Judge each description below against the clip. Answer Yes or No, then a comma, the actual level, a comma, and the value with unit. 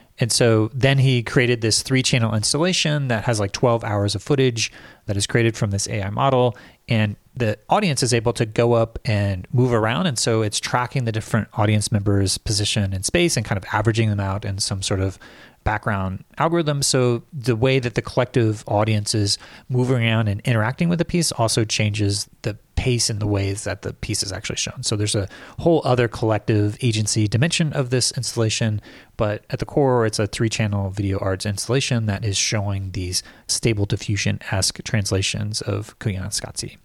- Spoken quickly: No, average, 190 wpm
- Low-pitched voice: Yes, low, 110 Hz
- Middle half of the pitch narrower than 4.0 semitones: Yes, average, 3.3 semitones